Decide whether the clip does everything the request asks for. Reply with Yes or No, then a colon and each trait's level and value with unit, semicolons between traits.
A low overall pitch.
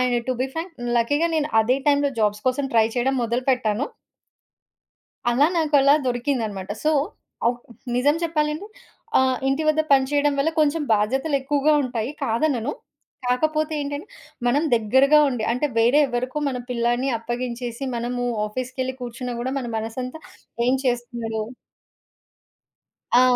No: very high, 255 Hz